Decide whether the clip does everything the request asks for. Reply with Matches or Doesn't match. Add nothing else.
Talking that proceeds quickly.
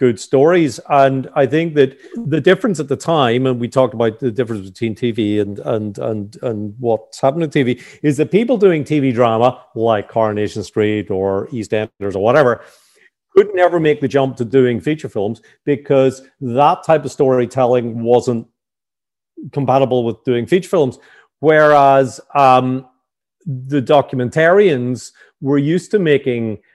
Doesn't match